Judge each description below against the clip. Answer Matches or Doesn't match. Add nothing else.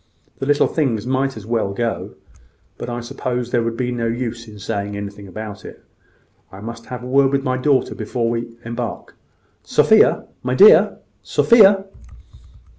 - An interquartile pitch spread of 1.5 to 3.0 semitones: Matches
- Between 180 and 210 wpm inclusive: Doesn't match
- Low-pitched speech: Matches